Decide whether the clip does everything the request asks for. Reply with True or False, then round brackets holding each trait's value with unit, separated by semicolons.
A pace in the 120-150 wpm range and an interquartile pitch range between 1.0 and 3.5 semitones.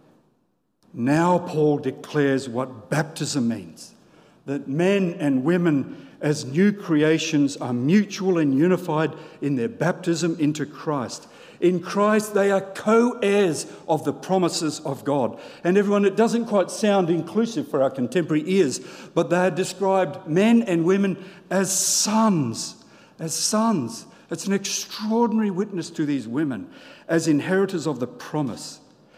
False (140 wpm; 4.7 semitones)